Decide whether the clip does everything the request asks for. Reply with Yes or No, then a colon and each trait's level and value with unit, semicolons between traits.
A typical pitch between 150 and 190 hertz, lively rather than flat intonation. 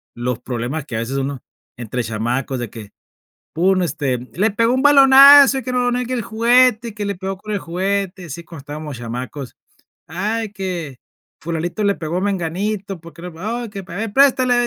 Yes: medium, 185 Hz; wide, 7.7 semitones